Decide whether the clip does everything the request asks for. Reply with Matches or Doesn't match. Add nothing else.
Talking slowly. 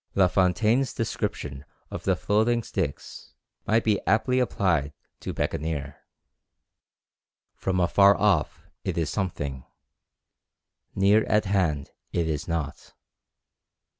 Matches